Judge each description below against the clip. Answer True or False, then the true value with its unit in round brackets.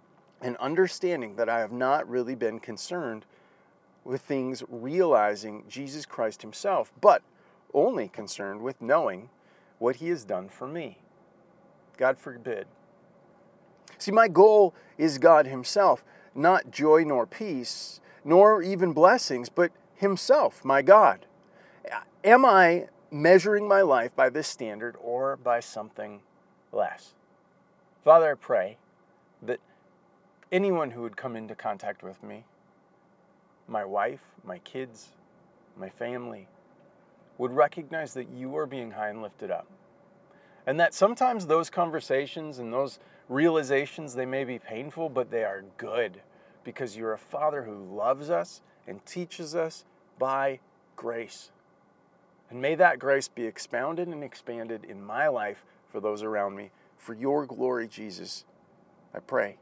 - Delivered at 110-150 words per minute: True (135 wpm)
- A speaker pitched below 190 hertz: True (135 Hz)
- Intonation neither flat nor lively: False (7.0 semitones)